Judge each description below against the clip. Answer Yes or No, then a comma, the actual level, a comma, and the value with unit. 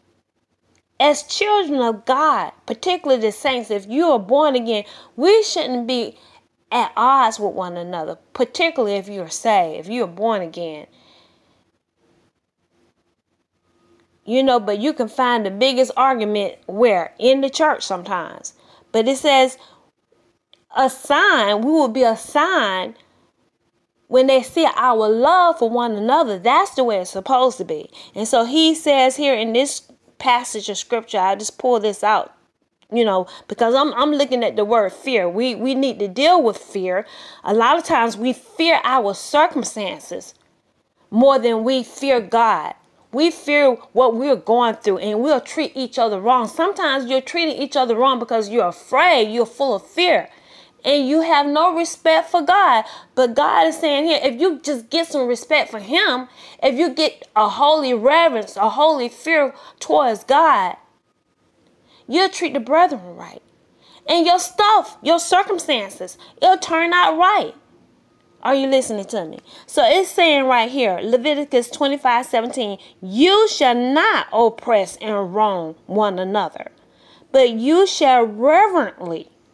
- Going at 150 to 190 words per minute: Yes, average, 160 wpm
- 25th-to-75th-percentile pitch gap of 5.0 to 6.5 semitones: Yes, wide, 5.5 semitones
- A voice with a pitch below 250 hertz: No, very high, 260 Hz